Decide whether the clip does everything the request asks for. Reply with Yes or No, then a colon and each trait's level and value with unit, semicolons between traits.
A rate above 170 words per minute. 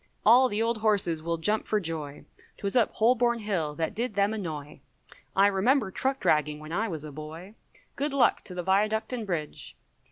Yes: average, 190 wpm